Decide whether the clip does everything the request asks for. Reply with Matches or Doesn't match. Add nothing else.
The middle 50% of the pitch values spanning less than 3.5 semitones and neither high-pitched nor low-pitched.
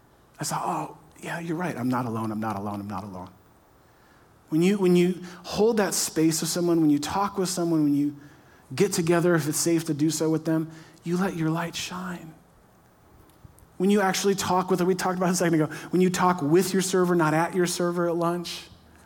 Matches